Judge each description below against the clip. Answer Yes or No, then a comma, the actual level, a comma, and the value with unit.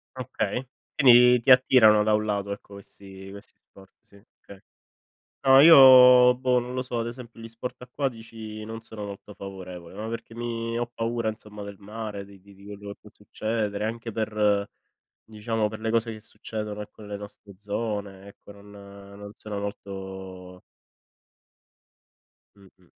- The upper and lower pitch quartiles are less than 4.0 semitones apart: Yes, narrow, 2.4 semitones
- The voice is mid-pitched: No, low, 105 Hz